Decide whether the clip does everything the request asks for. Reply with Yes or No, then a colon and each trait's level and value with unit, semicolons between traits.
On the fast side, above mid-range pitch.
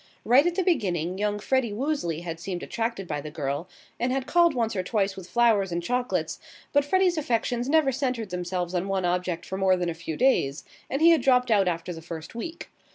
Yes: fast, 220 wpm; high, 205 Hz